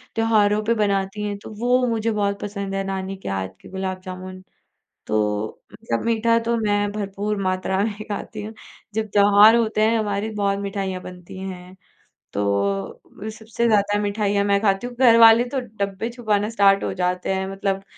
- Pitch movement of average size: No, narrow, 2.3 semitones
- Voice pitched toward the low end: No, high, 205 Hz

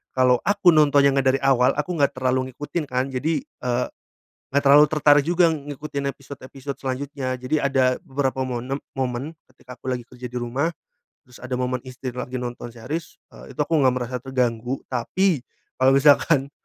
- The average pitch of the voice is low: Yes, low, 130 Hz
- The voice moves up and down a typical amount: No, narrow, 2.3 semitones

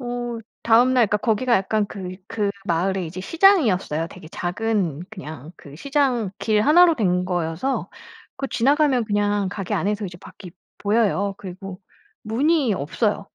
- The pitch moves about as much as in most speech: Yes, average, 4.8 semitones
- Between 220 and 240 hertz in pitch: No, high, 205 Hz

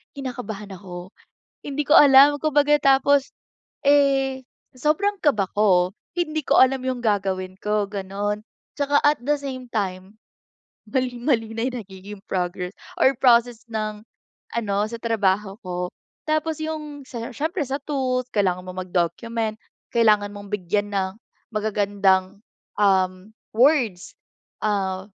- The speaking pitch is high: Yes, high, 220 Hz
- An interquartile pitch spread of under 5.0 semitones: No, wide, 5.5 semitones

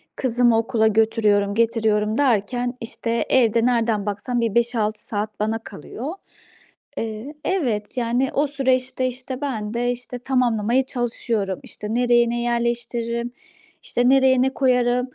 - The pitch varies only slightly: Yes, narrow, 2.3 semitones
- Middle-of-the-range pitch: No, high, 235 Hz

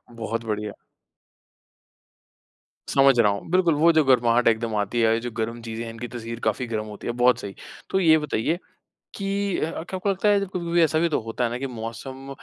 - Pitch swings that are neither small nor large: No, wide, 6.2 semitones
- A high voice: No, low, 120 Hz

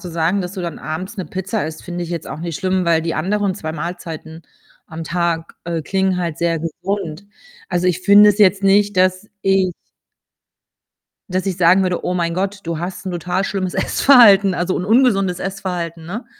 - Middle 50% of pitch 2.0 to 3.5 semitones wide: Yes, narrow, 2.5 semitones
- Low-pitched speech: No, medium, 180 Hz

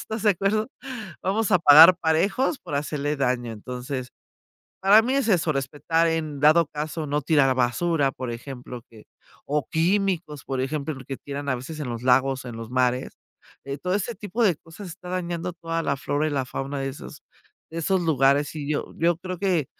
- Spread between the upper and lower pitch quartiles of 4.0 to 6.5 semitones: Yes, average, 4.5 semitones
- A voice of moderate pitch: Yes, medium, 150 Hz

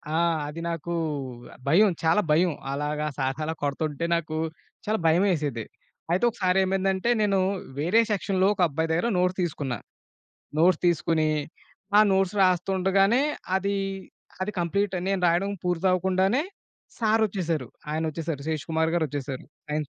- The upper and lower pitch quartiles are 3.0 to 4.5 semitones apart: Yes, average, 3.6 semitones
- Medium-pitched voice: Yes, medium, 175 Hz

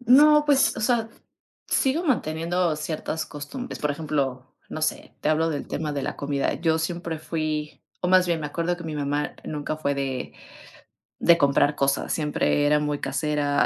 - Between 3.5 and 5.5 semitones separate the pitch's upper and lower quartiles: No, average, 2.9 semitones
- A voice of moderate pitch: Yes, medium, 155 Hz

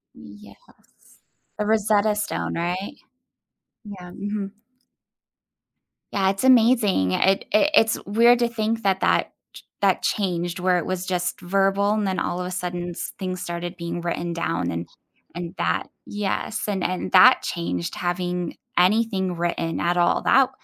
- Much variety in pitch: No, average, 3.1 semitones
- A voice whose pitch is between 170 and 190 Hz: Yes, medium, 185 Hz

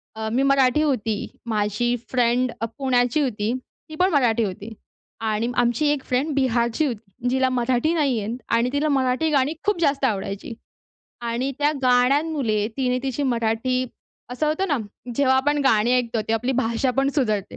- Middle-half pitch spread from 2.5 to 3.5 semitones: Yes, average, 3.2 semitones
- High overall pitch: Yes, very high, 250 Hz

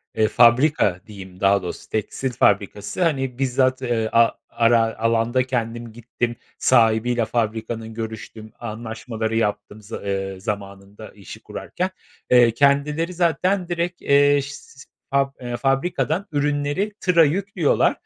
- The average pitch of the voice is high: No, low, 120 Hz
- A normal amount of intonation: Yes, average, 4.3 semitones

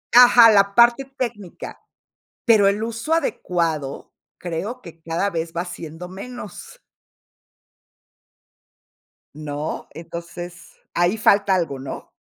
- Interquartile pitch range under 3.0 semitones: No, wide, 5.4 semitones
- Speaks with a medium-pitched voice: Yes, medium, 180 Hz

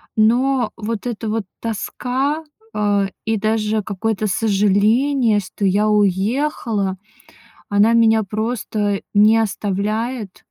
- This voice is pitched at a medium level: No, high, 215 Hz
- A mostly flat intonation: Yes, narrow, 2.0 semitones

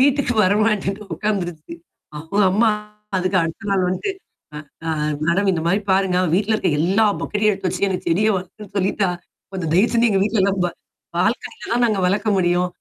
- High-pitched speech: Yes, high, 195 Hz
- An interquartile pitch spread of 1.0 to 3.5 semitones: Yes, average, 2.8 semitones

